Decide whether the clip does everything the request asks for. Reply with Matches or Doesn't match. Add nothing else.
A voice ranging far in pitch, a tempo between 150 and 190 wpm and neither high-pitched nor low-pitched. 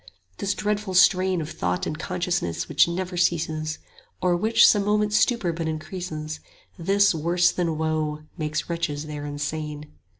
Doesn't match